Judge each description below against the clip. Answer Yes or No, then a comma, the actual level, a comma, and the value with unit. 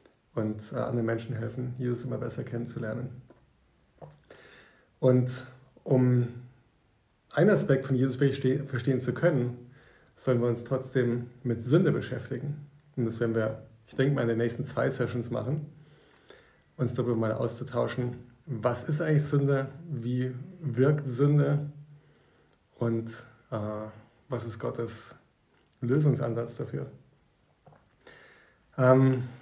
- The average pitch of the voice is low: Yes, low, 125 Hz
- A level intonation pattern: Yes, narrow, 2.3 semitones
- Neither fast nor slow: No, slow, 115 wpm